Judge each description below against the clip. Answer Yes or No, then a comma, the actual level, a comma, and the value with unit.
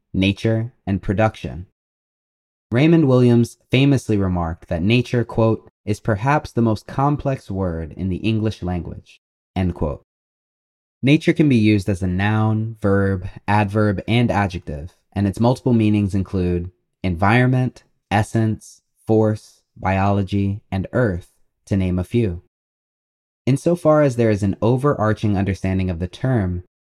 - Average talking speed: No, slow, 130 wpm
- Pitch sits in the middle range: No, low, 105 Hz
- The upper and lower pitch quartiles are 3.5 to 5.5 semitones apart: Yes, average, 4.2 semitones